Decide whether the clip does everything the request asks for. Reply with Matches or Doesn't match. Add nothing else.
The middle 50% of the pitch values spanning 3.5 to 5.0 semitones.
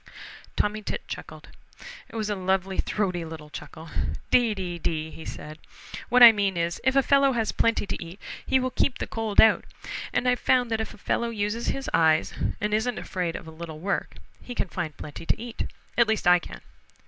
Doesn't match